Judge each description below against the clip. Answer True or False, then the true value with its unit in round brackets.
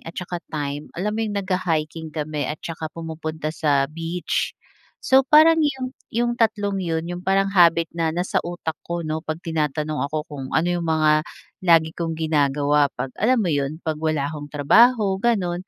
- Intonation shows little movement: False (3.7 semitones)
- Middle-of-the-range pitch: True (165 Hz)